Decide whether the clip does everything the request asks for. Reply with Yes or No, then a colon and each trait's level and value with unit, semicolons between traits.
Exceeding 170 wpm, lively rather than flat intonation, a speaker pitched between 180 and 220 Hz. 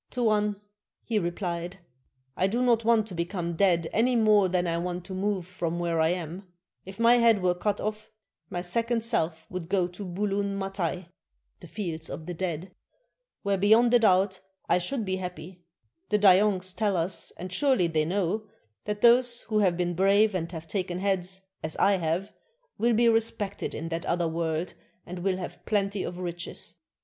No: average, 180 wpm; average, 3.3 semitones; medium, 185 Hz